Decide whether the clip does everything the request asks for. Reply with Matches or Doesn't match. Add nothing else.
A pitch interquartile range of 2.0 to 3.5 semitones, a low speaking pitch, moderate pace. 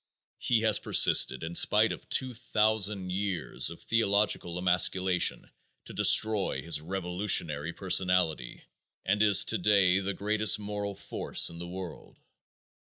Doesn't match